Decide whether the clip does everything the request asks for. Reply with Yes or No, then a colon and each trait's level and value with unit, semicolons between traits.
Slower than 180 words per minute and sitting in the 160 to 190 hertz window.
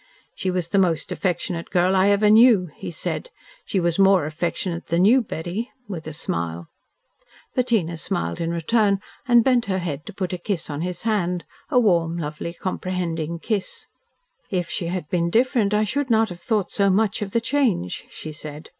No: average, 185 wpm; medium, 185 Hz